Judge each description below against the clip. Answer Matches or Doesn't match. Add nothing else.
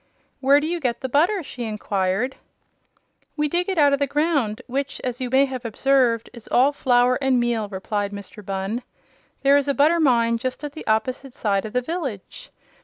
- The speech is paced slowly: Doesn't match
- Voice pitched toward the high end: Matches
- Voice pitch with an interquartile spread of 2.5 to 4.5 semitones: Matches